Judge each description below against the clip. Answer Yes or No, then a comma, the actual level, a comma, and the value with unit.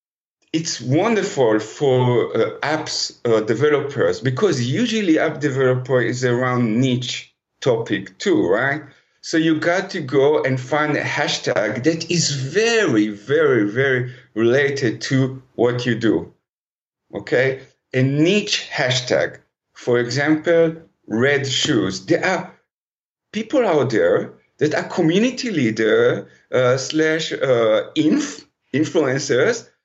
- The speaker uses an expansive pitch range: Yes, wide, 8.7 semitones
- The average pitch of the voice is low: No, medium, 150 Hz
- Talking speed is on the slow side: Yes, slow, 115 wpm